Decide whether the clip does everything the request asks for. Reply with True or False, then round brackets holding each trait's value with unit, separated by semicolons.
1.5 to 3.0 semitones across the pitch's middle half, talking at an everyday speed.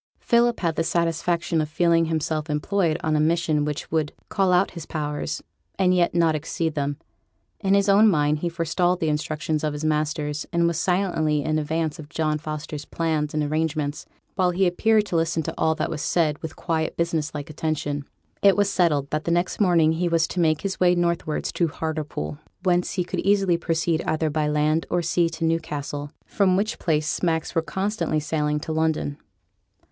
True (2.4 semitones; 195 wpm)